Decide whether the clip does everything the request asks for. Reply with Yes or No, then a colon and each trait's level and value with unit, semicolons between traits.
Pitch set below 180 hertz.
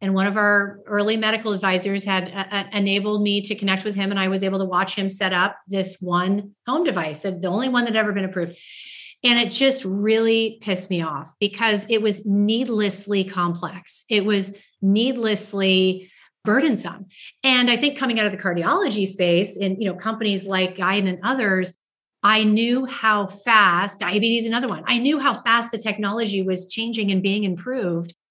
No: high, 200 Hz